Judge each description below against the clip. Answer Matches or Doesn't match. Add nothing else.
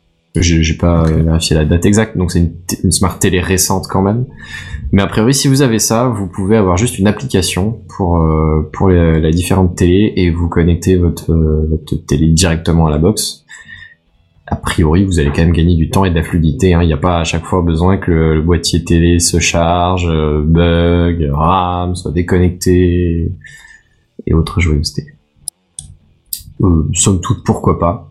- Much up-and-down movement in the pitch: Doesn't match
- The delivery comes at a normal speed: Matches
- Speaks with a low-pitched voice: Matches